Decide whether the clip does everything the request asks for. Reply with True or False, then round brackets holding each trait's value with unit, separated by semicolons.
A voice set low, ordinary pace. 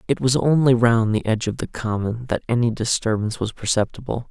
True (115 Hz; 195 wpm)